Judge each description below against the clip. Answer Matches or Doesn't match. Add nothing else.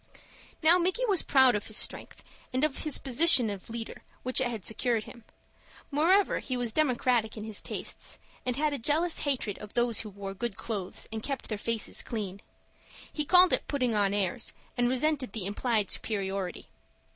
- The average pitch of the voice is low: Doesn't match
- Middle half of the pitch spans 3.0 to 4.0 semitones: Doesn't match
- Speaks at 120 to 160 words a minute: Doesn't match